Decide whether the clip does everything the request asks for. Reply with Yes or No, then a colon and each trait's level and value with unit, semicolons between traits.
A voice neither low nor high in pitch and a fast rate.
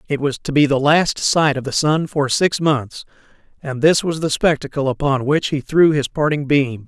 Yes: medium, 145 Hz; fast, 220 wpm